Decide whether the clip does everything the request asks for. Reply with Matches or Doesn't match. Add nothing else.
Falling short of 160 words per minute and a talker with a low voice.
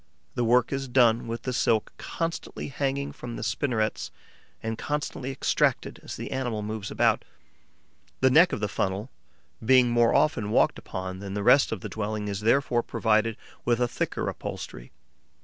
Doesn't match